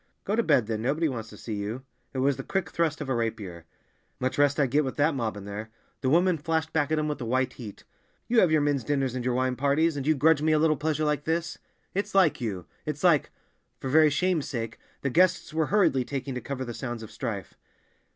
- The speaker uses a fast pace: Yes, fast, 240 wpm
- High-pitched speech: No, medium, 140 Hz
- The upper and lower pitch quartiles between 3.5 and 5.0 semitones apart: Yes, average, 4.4 semitones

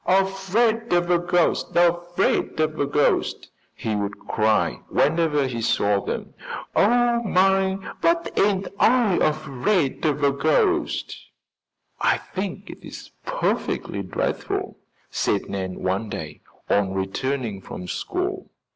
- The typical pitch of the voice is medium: Yes, medium, 170 Hz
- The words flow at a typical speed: No, slow, 120 wpm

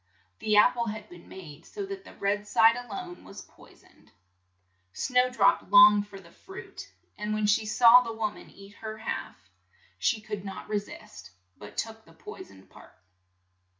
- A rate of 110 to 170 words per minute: No, average, 185 wpm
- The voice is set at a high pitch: Yes, high, 210 Hz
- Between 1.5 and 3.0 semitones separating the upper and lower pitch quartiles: Yes, narrow, 2.4 semitones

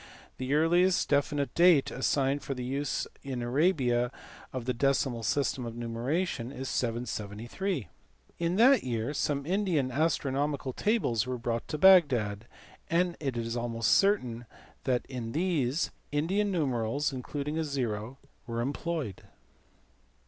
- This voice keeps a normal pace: No, slow, 130 wpm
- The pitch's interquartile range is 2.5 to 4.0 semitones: No, average, 5.0 semitones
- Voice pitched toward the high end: No, low, 135 Hz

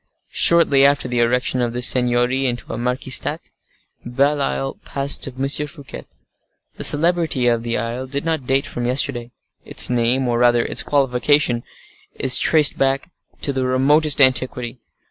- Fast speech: No, average, 155 wpm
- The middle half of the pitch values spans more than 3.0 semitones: No, narrow, 2.4 semitones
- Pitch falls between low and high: No, low, 130 Hz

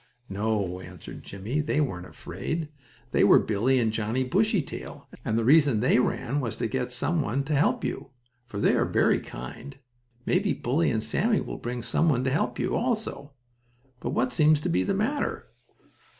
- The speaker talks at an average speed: Yes, average, 180 wpm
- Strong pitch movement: Yes, wide, 5.9 semitones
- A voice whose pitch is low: Yes, low, 130 Hz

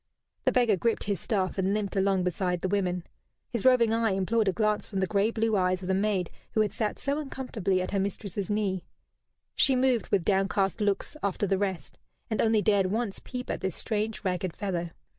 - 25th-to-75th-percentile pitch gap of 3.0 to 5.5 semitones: No, narrow, 2.6 semitones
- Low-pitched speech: No, high, 200 Hz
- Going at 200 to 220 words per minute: Yes, fast, 205 wpm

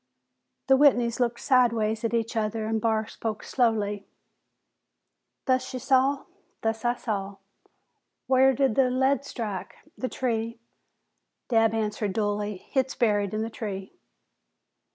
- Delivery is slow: Yes, slow, 130 wpm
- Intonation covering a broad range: No, average, 3.1 semitones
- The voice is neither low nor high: No, high, 225 Hz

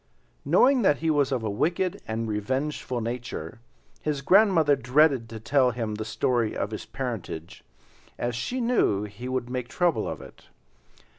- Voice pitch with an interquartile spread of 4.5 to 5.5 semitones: Yes, average, 5.2 semitones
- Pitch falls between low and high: No, low, 125 Hz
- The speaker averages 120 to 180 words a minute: Yes, average, 160 wpm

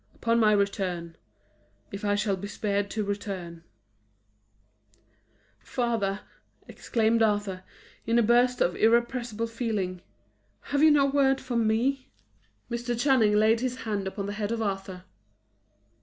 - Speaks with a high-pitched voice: Yes, high, 215 Hz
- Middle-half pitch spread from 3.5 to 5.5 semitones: No, average, 3.1 semitones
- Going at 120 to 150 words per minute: Yes, slow, 135 wpm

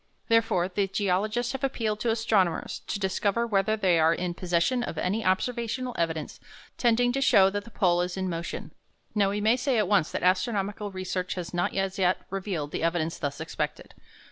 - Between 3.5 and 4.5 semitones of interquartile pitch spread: Yes, average, 3.9 semitones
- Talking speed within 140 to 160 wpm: No, average, 190 wpm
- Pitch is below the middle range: No, high, 195 Hz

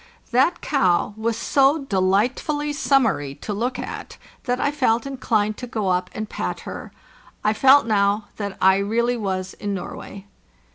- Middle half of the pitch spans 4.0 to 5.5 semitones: Yes, average, 4.6 semitones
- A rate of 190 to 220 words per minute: No, average, 160 wpm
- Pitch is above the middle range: Yes, high, 220 Hz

